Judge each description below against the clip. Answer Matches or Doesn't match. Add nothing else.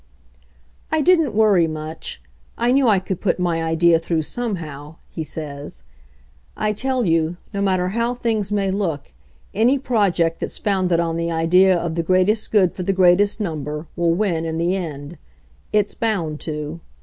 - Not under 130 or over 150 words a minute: Doesn't match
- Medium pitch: Matches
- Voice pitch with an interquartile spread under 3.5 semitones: Doesn't match